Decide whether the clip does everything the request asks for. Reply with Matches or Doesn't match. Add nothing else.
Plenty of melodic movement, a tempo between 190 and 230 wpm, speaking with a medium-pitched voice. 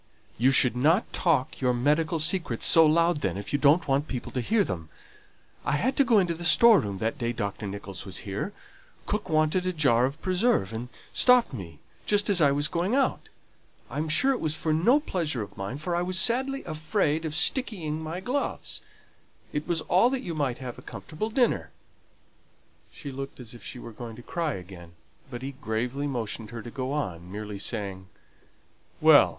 Matches